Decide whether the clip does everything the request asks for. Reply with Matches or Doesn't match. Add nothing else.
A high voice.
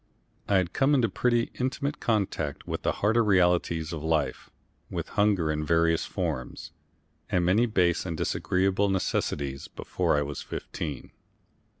Doesn't match